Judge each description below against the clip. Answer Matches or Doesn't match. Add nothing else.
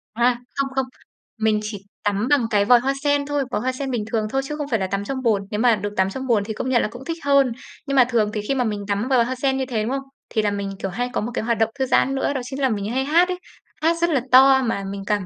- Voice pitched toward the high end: Matches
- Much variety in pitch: Doesn't match